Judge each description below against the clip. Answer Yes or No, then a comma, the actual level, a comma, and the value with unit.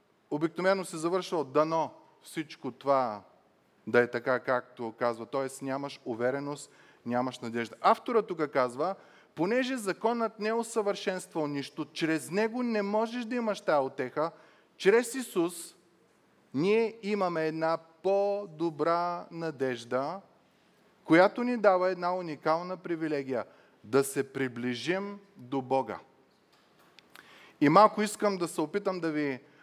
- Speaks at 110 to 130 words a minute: Yes, average, 120 wpm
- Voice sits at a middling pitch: Yes, medium, 165 Hz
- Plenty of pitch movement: Yes, wide, 6.6 semitones